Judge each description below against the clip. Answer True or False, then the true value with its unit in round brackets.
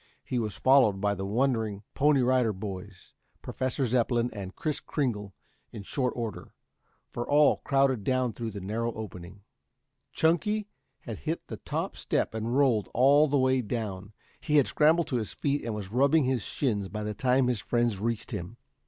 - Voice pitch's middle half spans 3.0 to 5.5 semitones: True (4.3 semitones)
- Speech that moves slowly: False (175 wpm)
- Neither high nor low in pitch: False (120 Hz)